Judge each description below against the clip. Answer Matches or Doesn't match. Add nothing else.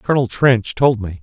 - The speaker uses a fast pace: Doesn't match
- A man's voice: Matches